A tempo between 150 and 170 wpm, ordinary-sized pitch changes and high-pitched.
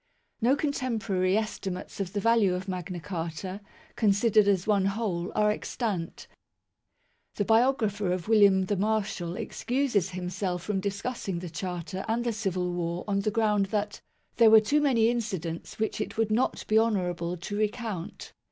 Yes: average, 160 wpm; average, 3.4 semitones; high, 200 Hz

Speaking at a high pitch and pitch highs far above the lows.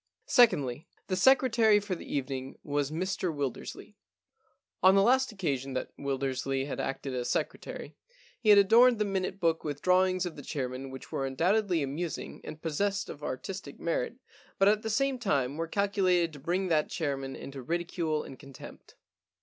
No: medium, 165 Hz; wide, 6.2 semitones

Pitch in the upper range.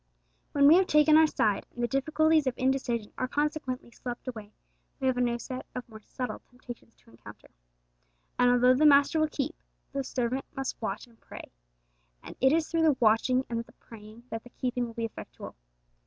Yes: very high, 255 Hz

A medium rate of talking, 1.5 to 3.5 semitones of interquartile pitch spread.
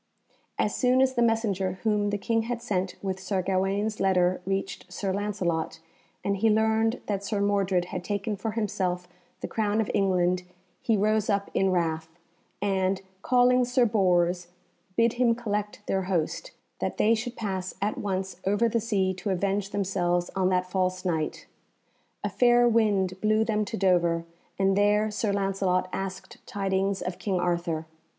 Yes: average, 165 wpm; average, 2.7 semitones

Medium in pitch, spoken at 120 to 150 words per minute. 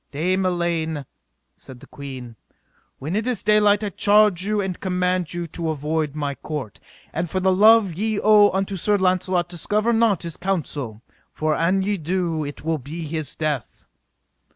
No: medium, 175 Hz; average, 170 wpm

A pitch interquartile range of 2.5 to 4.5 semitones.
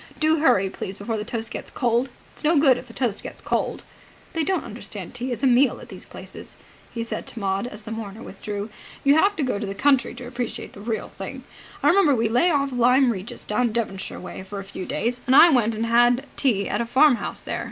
Yes: average, 4.0 semitones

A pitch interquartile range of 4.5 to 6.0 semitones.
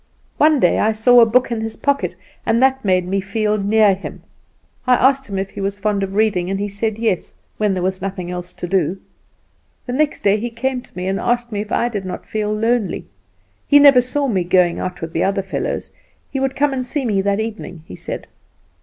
No: average, 4.1 semitones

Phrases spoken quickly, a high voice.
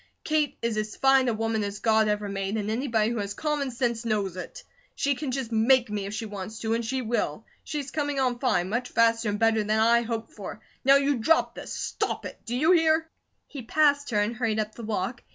Yes: fast, 230 wpm; high, 230 Hz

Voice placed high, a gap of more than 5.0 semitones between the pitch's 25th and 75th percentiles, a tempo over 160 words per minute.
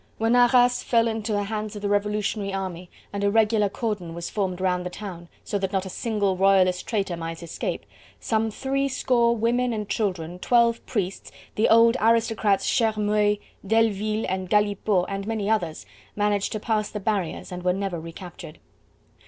No: high, 205 Hz; average, 2.9 semitones; average, 170 wpm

